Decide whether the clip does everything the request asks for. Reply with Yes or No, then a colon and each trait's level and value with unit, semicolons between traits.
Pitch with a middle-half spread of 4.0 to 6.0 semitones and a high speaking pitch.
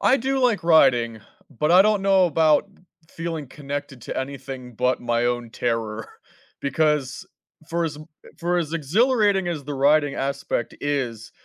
No: average, 5.2 semitones; medium, 145 Hz